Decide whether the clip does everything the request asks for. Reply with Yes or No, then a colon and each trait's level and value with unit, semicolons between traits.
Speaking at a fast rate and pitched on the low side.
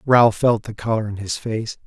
Yes: fast, 225 wpm; low, 110 Hz